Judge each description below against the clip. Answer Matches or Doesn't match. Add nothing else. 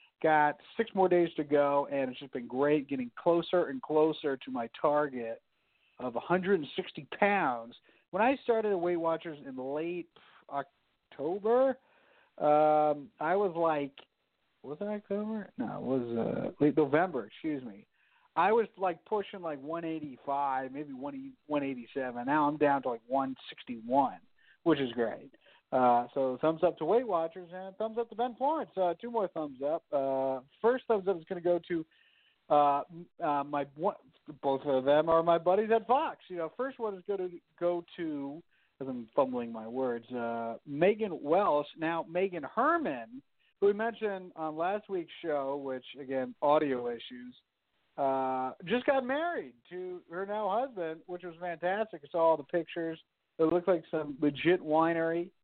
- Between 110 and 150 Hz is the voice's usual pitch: Doesn't match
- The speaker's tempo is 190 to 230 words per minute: Doesn't match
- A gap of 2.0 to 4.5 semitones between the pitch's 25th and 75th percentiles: Doesn't match